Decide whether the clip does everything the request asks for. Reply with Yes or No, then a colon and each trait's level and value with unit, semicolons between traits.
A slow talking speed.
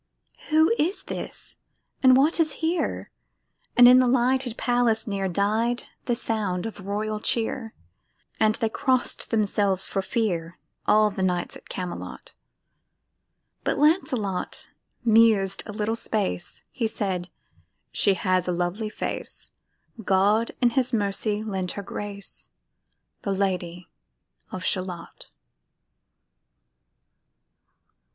Yes: slow, 115 wpm